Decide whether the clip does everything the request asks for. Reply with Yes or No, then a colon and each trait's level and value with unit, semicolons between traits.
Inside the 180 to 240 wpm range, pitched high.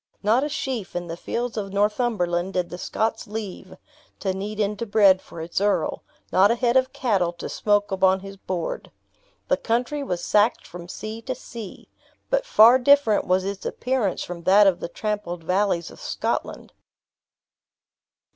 No: average, 165 wpm; high, 205 Hz